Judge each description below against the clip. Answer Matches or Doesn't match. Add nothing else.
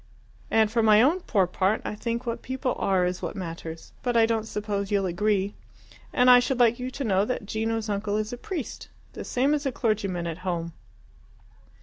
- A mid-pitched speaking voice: Doesn't match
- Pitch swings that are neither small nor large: Matches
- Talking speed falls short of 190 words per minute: Doesn't match